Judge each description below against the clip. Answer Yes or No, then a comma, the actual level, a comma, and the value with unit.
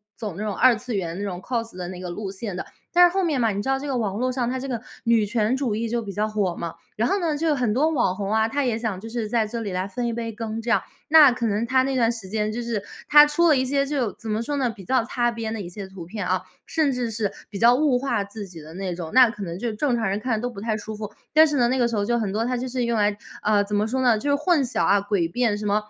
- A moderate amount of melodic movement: Yes, average, 3.5 semitones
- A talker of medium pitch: No, high, 230 Hz